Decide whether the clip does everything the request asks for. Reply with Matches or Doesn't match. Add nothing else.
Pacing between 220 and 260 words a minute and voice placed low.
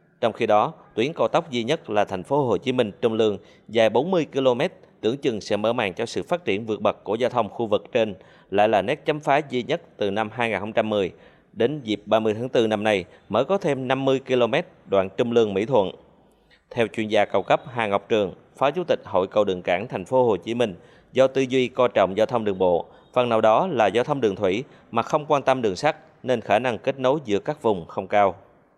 Matches